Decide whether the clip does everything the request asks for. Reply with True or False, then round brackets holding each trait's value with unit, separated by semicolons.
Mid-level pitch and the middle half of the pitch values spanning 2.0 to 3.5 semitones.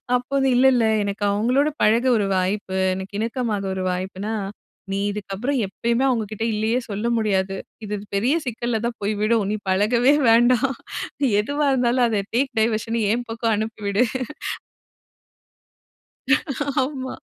False (225 Hz; 3.2 semitones)